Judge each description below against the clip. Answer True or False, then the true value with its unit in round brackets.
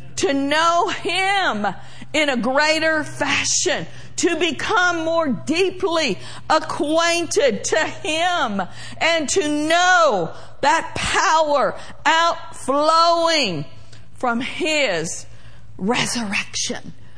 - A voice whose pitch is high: True (320 Hz)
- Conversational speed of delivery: False (80 wpm)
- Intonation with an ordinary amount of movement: True (4.5 semitones)